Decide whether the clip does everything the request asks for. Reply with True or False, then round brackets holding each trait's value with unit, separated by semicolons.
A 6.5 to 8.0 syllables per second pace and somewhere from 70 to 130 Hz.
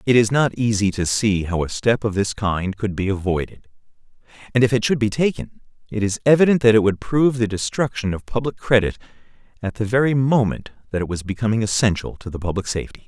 False (6.0 syllables/s; 110 Hz)